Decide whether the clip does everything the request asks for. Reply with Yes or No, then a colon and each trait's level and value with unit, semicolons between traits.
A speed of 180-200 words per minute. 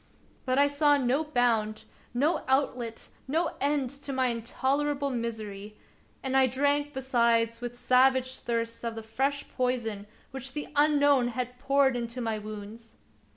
No: average, 145 wpm